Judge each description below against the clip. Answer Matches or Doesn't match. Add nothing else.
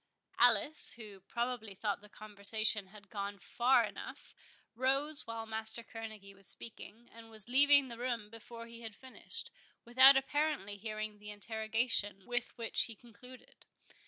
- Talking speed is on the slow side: Doesn't match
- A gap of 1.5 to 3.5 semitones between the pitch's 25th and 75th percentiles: Matches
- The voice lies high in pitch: Matches